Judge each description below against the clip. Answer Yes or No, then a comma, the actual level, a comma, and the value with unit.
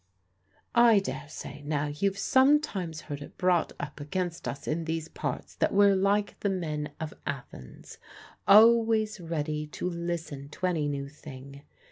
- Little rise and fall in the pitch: No, average, 5.0 semitones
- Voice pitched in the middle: Yes, medium, 165 Hz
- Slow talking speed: No, average, 145 wpm